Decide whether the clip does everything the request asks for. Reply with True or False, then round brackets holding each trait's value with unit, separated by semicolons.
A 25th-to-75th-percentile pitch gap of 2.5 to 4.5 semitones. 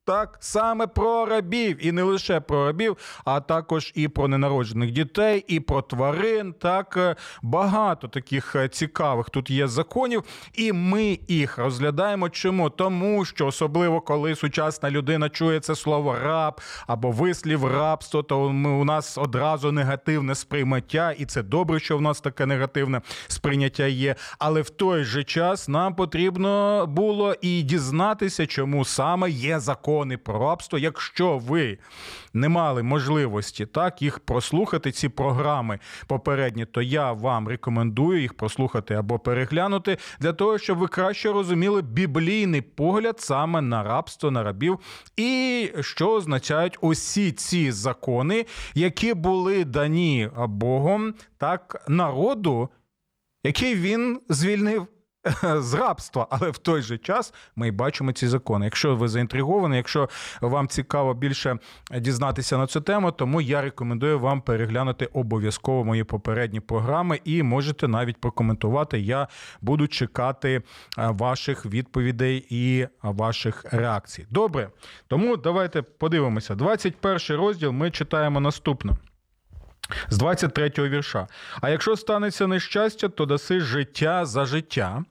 False (5.3 semitones)